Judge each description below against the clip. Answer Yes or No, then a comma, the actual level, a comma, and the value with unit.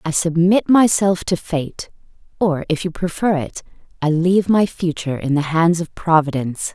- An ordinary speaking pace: Yes, average, 170 wpm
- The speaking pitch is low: No, medium, 170 Hz